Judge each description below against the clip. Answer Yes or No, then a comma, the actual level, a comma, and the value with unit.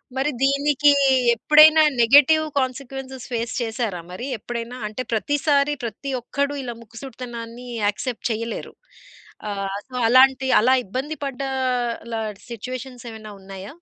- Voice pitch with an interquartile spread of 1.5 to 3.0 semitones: No, average, 3.4 semitones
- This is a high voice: Yes, very high, 250 Hz